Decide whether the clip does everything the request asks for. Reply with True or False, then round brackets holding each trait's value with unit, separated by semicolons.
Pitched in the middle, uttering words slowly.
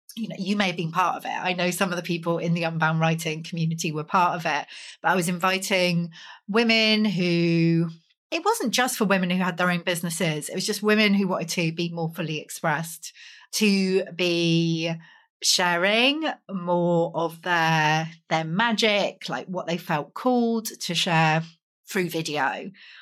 False (175 Hz; 175 wpm)